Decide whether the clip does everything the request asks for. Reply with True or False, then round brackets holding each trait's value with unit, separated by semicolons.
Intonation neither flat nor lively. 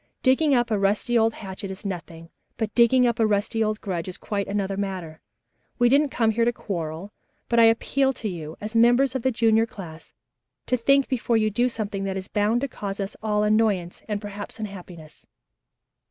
True (3.2 semitones)